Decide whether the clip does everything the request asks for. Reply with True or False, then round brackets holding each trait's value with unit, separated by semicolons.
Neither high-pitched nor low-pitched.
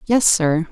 True (180 Hz)